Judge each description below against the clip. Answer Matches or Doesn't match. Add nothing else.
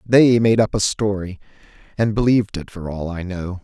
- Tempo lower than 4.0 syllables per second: Doesn't match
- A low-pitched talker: Matches